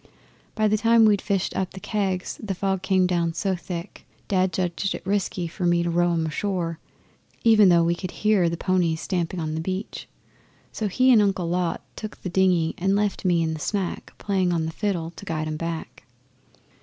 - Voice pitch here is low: No, medium, 185 Hz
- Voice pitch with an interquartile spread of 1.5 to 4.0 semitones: Yes, average, 2.8 semitones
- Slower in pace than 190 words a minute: No, fast, 205 wpm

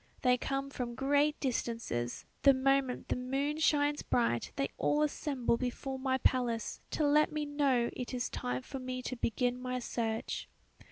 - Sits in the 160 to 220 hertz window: No, very high, 255 Hz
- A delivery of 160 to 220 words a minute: Yes, average, 165 wpm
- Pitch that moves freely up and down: No, narrow, 2.6 semitones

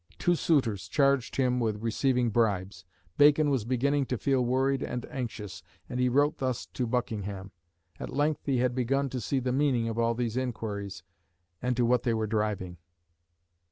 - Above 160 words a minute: Yes, average, 175 wpm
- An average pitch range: Yes, average, 3.3 semitones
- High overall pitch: No, low, 125 Hz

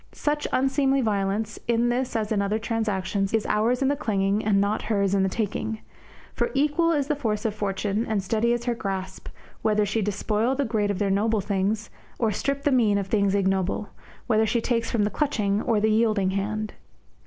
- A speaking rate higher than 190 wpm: Yes, average, 200 wpm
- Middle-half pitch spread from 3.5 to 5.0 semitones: No, average, 2.8 semitones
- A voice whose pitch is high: Yes, high, 215 Hz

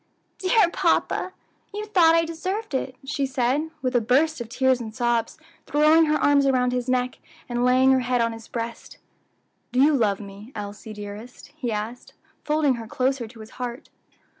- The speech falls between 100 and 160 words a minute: No, average, 180 wpm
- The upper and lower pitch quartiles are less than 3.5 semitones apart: No, average, 4.3 semitones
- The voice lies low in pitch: No, very high, 255 Hz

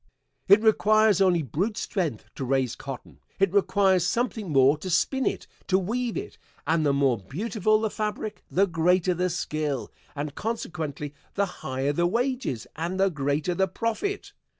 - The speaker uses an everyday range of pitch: No, wide, 6.4 semitones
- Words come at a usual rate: Yes, average, 160 wpm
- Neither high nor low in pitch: Yes, medium, 180 Hz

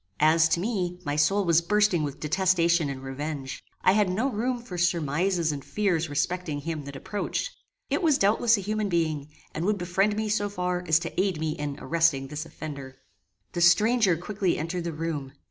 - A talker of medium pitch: Yes, medium, 170 Hz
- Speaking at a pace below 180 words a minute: No, average, 190 wpm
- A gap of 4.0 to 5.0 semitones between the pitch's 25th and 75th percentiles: Yes, average, 4.6 semitones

